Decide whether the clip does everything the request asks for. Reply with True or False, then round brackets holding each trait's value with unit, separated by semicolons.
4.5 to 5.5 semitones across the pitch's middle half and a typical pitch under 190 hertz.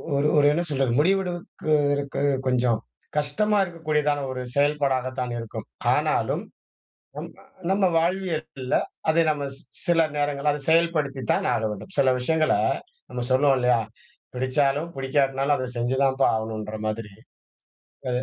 False (3.3 semitones; 140 Hz)